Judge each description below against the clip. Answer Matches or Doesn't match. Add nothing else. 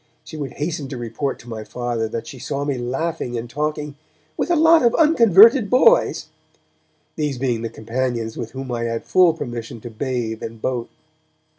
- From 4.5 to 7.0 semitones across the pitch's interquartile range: Matches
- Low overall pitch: Matches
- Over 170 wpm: Matches